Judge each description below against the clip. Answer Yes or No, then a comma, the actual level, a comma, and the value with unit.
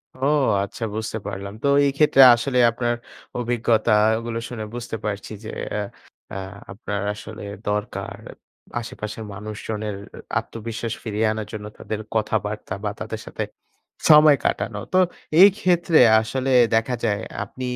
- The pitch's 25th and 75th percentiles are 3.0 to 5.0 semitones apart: No, narrow, 2.5 semitones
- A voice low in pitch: Yes, low, 110 Hz